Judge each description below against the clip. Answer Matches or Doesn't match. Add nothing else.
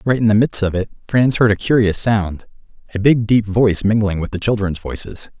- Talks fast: Matches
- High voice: Doesn't match